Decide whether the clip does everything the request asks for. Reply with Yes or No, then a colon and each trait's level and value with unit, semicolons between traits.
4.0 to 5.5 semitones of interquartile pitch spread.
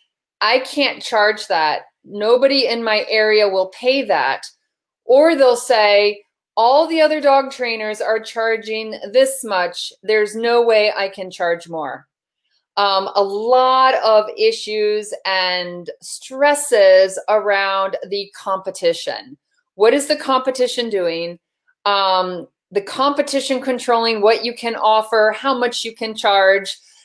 Yes: average, 5.1 semitones